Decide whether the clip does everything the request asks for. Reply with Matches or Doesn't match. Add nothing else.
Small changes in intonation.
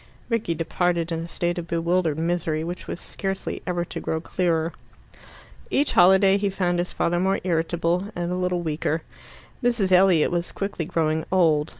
Matches